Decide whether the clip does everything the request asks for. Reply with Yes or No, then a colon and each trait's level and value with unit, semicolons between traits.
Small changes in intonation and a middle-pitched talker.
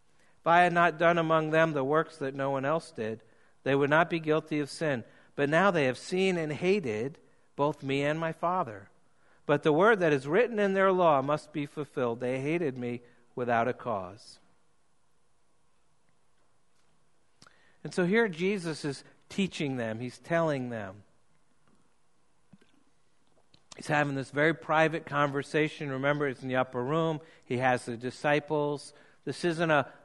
No: average, 3.6 semitones; medium, 150 Hz